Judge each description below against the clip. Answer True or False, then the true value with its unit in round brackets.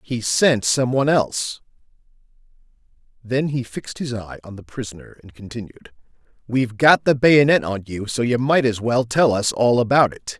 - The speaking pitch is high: False (120 Hz)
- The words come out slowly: False (175 wpm)